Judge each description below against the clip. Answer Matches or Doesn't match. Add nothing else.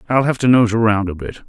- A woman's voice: Doesn't match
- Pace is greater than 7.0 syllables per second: Doesn't match